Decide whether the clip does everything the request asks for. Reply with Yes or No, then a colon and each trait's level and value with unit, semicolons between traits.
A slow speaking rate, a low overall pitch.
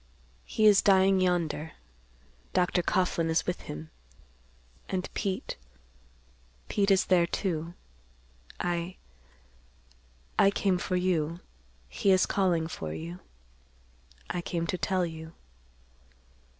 No: slow, 100 wpm; medium, 160 Hz